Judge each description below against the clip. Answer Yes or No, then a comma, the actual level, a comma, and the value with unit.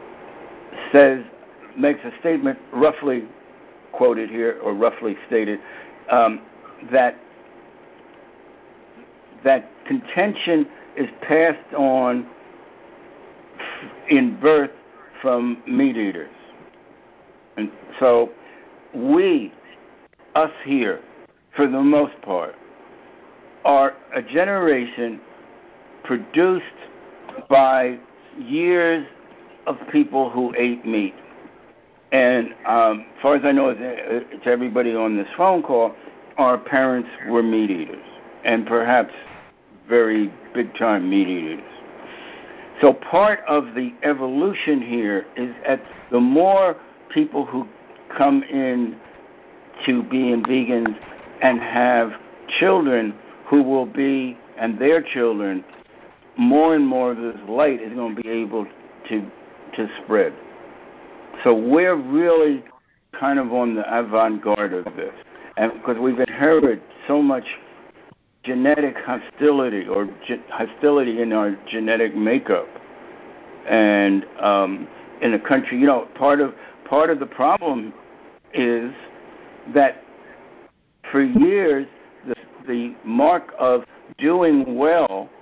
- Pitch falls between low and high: No, low, 130 Hz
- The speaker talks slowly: Yes, slow, 110 wpm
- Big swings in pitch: No, average, 4.6 semitones